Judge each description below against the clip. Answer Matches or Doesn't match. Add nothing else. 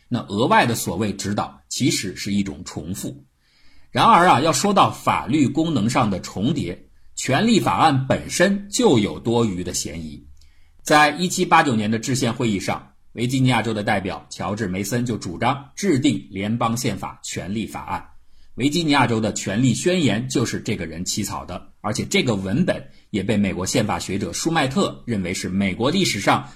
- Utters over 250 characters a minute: Matches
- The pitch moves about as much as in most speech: Doesn't match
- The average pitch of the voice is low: Matches